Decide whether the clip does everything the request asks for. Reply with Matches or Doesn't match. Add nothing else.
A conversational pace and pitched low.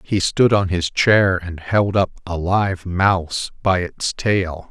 Matches